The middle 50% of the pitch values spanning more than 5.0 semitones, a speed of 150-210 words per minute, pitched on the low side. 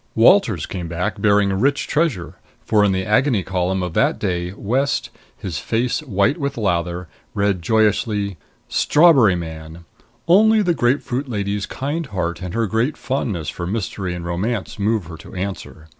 Yes: wide, 5.4 semitones; average, 160 wpm; low, 100 Hz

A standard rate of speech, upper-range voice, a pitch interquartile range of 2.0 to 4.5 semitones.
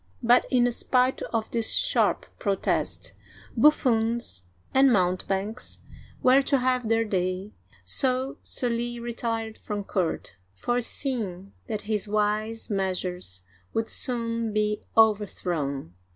No: slow, 115 wpm; high, 220 Hz; average, 3.9 semitones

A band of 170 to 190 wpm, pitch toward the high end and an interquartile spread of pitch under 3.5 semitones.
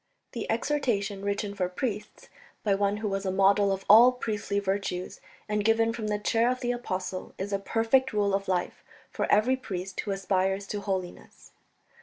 Yes: average, 180 wpm; high, 200 Hz; narrow, 2.5 semitones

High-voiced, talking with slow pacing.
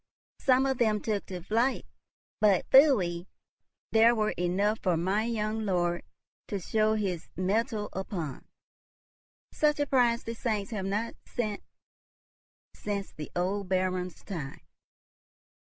Yes: high, 205 Hz; slow, 125 wpm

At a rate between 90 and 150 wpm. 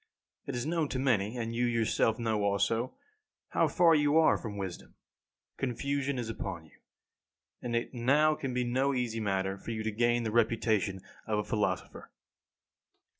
No: average, 170 wpm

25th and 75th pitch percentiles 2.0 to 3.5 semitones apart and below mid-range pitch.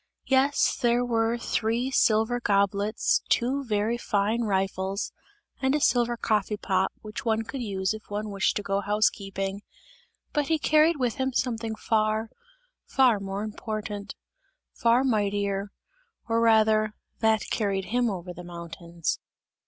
No: average, 3.1 semitones; high, 215 Hz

